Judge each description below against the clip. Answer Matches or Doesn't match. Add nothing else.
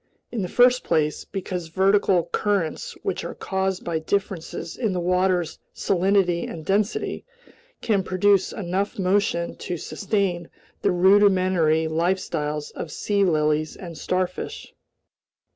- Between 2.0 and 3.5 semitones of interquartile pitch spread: Matches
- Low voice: Doesn't match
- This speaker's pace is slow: Matches